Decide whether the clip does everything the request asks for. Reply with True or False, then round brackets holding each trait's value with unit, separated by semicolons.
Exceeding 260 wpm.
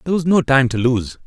True (285 wpm)